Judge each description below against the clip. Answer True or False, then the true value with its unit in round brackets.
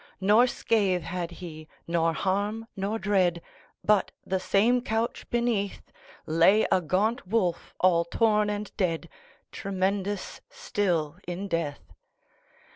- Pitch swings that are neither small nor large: True (3.5 semitones)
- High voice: True (195 Hz)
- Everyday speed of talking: False (105 wpm)